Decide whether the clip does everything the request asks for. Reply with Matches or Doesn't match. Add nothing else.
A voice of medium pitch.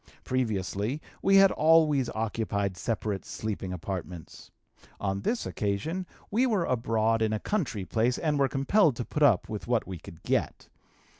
Doesn't match